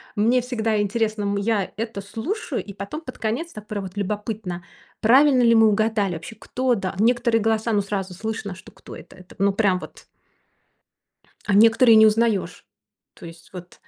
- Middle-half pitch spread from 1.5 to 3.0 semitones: Yes, narrow, 2.4 semitones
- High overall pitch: Yes, high, 215 Hz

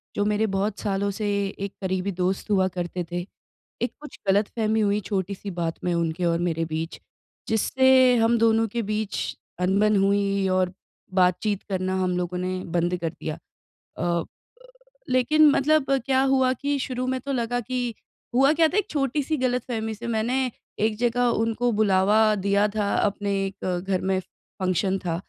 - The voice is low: No, high, 210 Hz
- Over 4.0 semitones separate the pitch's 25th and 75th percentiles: Yes, average, 4.7 semitones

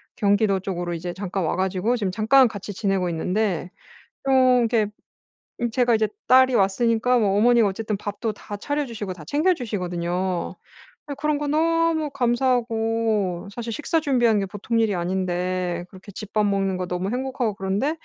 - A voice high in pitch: Yes, high, 215 Hz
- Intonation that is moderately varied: Yes, average, 4.5 semitones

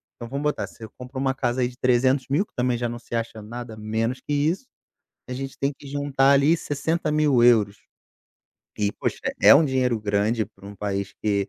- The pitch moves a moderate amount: Yes, average, 3.9 semitones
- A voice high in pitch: No, low, 125 Hz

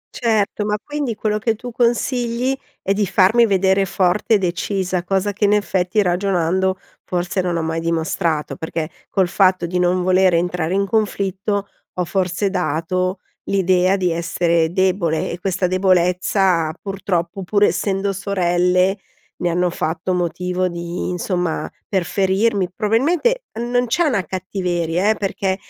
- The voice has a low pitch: No, medium, 185 Hz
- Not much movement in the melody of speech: Yes, narrow, 2.3 semitones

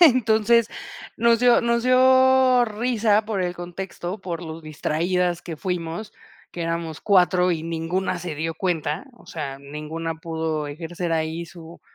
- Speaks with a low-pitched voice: No, medium, 175 Hz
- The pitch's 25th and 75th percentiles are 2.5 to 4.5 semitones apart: No, average, 5.1 semitones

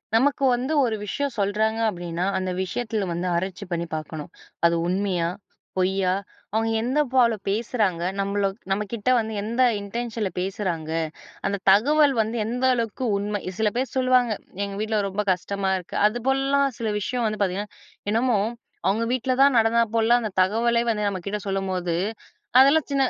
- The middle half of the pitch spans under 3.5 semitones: No, average, 3.9 semitones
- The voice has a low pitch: No, high, 215 Hz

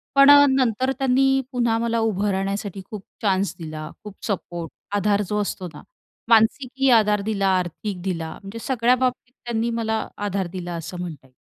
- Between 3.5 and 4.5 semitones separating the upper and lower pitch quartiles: Yes, average, 3.9 semitones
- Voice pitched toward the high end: Yes, high, 210 Hz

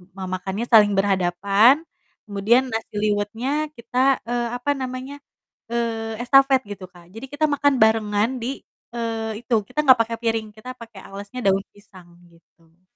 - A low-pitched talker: No, high, 225 Hz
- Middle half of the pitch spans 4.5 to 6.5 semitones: No, average, 3.3 semitones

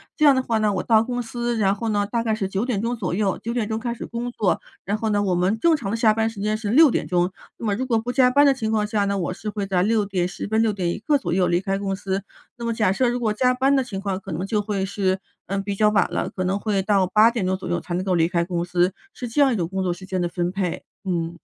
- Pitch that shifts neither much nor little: Yes, average, 3.4 semitones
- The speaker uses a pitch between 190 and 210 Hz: Yes, high, 205 Hz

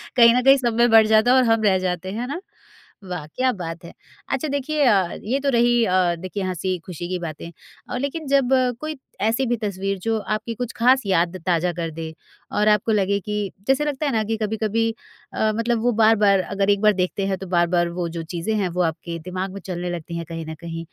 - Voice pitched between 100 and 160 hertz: No, high, 205 Hz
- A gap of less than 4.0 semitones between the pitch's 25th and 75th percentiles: No, average, 5.1 semitones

